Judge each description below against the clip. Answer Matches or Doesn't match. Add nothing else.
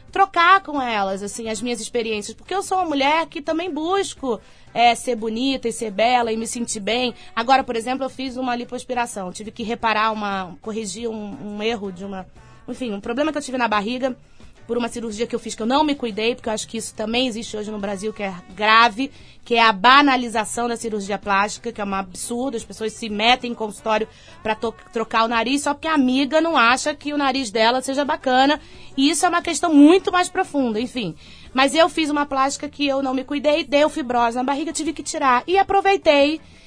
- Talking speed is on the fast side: Matches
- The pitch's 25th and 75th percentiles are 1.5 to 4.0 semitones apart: Doesn't match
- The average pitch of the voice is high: Matches